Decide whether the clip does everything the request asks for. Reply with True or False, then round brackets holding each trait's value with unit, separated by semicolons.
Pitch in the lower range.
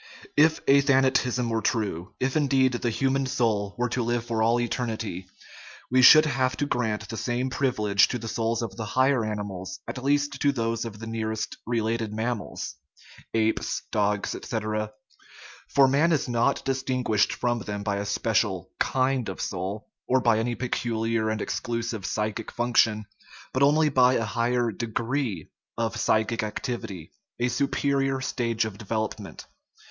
True (115 Hz)